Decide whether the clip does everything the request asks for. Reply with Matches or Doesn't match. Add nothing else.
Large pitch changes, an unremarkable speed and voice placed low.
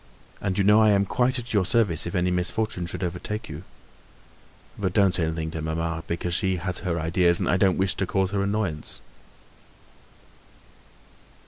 Doesn't match